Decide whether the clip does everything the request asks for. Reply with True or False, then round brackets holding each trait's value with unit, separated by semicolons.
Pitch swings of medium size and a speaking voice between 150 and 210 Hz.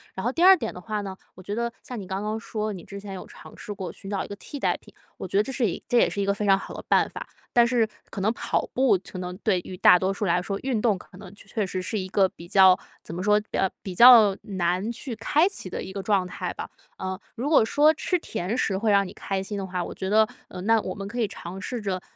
True (3.2 semitones; 200 Hz)